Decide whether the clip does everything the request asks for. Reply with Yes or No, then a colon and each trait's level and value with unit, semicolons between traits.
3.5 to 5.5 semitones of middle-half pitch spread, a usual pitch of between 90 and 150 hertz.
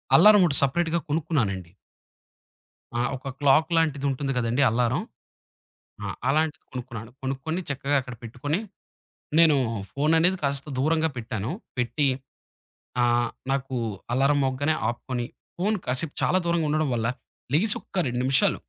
Yes: average, 4.2 semitones; medium, 140 Hz